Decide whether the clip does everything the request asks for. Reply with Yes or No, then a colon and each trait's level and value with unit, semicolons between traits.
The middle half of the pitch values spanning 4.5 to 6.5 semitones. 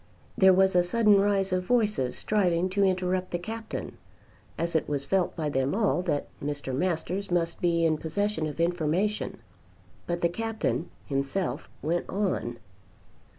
No: average, 3.6 semitones